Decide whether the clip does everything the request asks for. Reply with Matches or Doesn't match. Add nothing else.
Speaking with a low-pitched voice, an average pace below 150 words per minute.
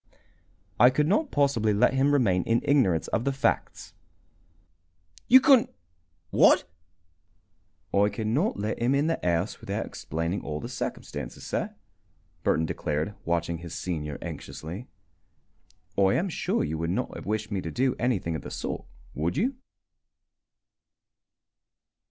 Matches